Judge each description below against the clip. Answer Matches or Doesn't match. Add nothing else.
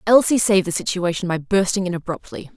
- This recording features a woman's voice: Matches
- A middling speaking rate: Matches